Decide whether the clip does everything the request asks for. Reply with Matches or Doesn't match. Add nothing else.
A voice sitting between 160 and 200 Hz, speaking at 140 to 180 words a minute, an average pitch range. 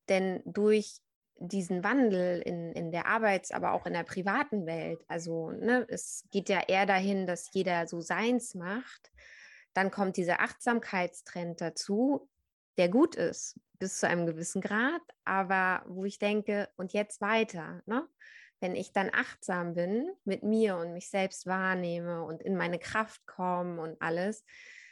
Matches